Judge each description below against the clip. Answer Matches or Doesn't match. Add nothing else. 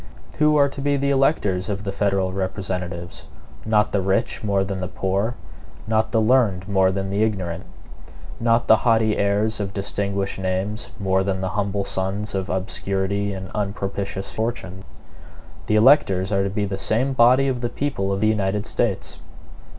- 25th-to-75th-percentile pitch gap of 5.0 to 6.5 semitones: Doesn't match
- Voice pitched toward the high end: Doesn't match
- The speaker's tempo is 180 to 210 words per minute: Doesn't match